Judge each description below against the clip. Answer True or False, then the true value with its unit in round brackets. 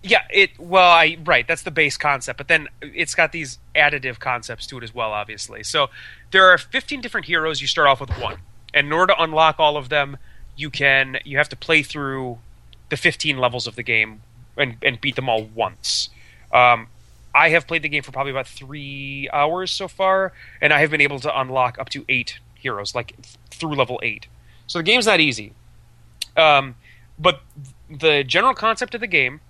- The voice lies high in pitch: False (140 Hz)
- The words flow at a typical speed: False (210 wpm)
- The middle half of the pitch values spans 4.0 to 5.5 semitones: True (4.8 semitones)